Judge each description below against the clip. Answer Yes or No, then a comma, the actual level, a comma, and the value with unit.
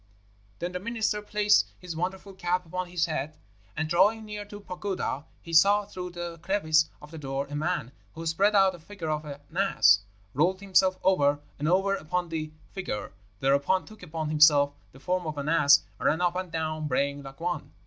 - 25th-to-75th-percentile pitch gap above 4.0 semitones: No, average, 3.7 semitones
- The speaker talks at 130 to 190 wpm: No, average, 200 wpm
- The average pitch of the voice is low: No, medium, 170 Hz